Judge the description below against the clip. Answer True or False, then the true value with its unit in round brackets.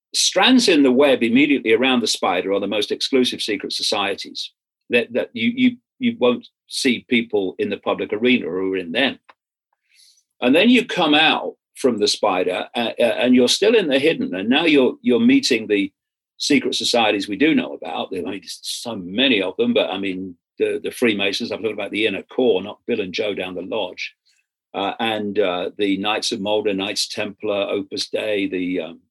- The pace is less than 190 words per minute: False (200 wpm)